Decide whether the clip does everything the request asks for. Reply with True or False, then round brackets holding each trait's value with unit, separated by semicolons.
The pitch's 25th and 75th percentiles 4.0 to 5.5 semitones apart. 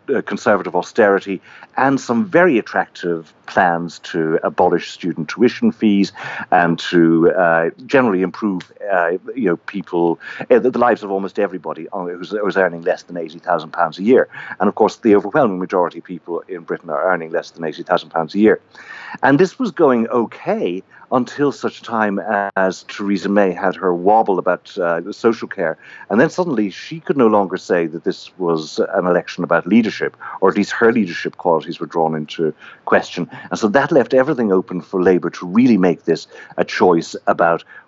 True (5.0 semitones)